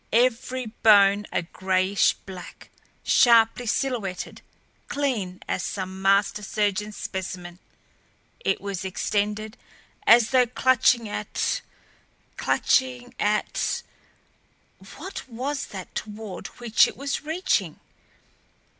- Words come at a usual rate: No, slow, 95 wpm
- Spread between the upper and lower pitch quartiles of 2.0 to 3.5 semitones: No, average, 4.2 semitones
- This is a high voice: Yes, high, 215 Hz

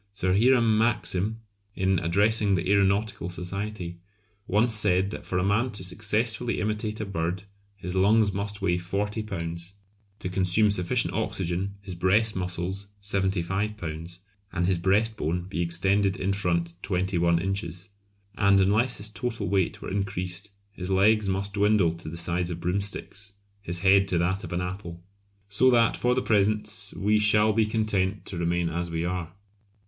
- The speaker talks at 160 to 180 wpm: Yes, average, 165 wpm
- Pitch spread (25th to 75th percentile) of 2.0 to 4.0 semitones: Yes, average, 3.0 semitones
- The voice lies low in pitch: Yes, very low, 95 Hz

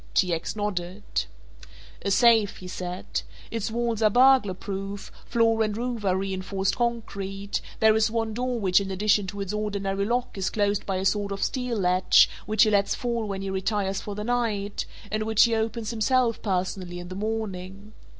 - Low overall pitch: No, high, 205 Hz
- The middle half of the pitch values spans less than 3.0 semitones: Yes, narrow, 2.5 semitones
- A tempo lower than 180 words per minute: No, average, 185 wpm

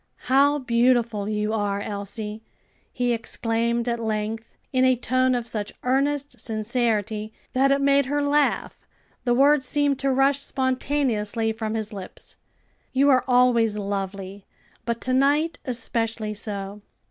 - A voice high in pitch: Yes, high, 235 Hz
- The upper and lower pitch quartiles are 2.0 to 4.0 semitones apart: Yes, average, 3.7 semitones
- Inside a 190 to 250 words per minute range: No, slow, 135 wpm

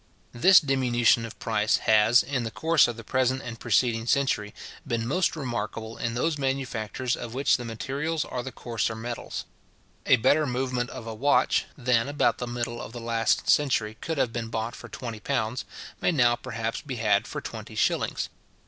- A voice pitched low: Yes, low, 120 Hz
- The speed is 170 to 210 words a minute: Yes, average, 185 wpm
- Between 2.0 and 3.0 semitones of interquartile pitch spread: Yes, average, 2.7 semitones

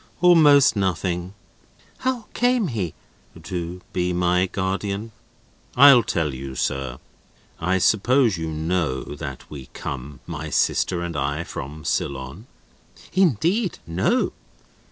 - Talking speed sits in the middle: No, slow, 115 wpm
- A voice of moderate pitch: No, very low, 90 Hz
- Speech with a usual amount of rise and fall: No, wide, 7.0 semitones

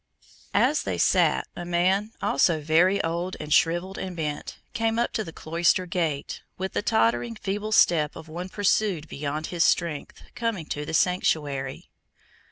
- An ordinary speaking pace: Yes, average, 160 wpm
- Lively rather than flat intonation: No, average, 3.8 semitones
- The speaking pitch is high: No, medium, 170 Hz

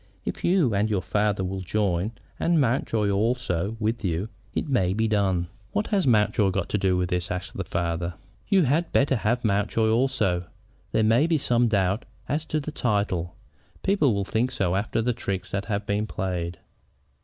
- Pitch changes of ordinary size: Yes, average, 4.5 semitones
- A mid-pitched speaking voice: No, low, 105 Hz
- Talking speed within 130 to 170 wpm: No, average, 185 wpm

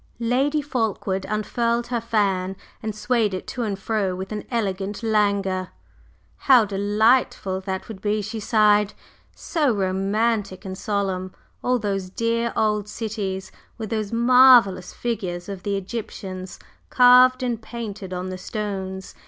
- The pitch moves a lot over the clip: No, average, 3.3 semitones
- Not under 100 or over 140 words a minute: Yes, slow, 135 wpm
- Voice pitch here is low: No, high, 210 Hz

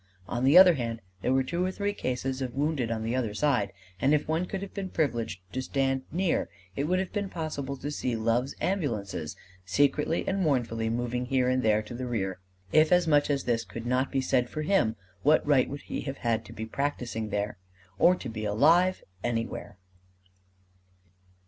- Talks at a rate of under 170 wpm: No, average, 200 wpm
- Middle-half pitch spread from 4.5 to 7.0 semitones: Yes, average, 5.1 semitones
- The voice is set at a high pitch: No, low, 130 Hz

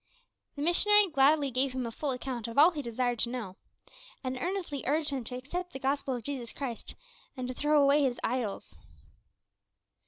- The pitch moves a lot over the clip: No, average, 3.0 semitones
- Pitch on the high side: Yes, very high, 270 Hz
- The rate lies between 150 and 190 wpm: Yes, average, 185 wpm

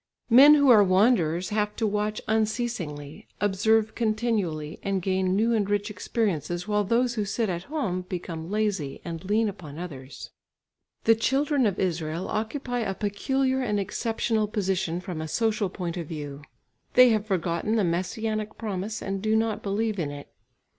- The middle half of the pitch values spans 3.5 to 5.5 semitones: Yes, average, 3.9 semitones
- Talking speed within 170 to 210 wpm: No, average, 160 wpm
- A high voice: Yes, high, 205 Hz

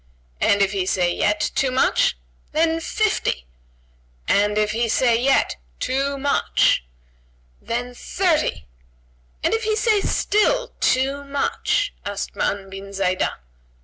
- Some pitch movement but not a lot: No, wide, 8.2 semitones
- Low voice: No, very high, 250 Hz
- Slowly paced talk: Yes, slow, 125 wpm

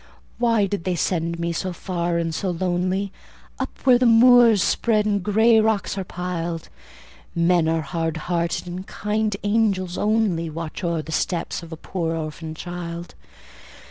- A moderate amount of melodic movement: Yes, average, 3.7 semitones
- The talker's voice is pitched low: No, medium, 180 Hz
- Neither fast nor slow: Yes, average, 160 wpm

